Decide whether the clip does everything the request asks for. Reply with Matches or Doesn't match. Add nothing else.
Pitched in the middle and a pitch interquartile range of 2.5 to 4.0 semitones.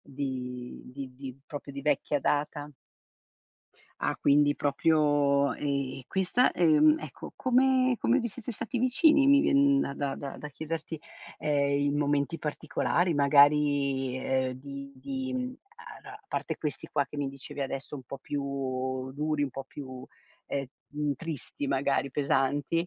Matches